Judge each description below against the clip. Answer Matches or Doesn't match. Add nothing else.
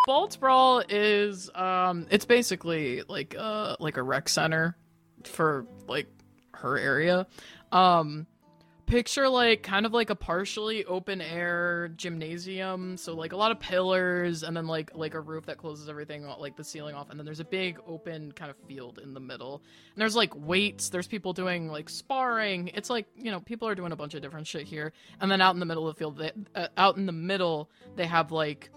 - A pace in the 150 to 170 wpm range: Doesn't match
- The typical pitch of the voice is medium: Matches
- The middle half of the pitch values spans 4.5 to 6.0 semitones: Doesn't match